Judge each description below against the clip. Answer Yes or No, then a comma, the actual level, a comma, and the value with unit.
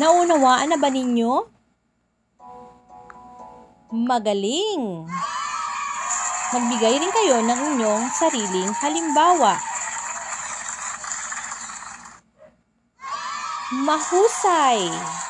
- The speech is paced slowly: Yes, slow, 55 wpm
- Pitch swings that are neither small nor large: No, wide, 7.5 semitones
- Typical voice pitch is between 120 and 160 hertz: No, very high, 250 Hz